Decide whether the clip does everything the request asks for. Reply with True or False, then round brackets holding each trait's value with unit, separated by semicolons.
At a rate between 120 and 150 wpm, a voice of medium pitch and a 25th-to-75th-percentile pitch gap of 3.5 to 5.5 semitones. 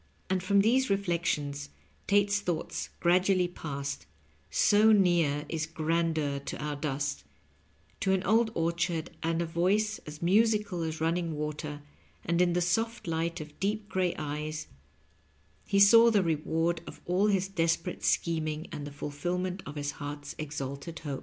False (160 wpm; 170 Hz; 4.1 semitones)